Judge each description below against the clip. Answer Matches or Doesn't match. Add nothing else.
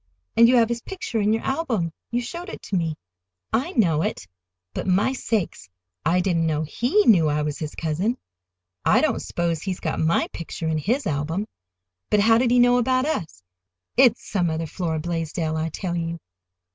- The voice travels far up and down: Matches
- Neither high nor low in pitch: Matches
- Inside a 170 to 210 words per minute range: Matches